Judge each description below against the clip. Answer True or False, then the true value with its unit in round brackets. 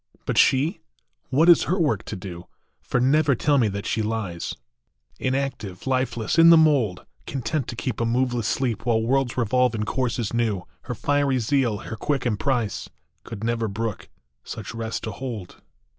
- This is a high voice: False (120 Hz)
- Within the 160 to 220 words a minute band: True (170 wpm)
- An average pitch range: True (3.6 semitones)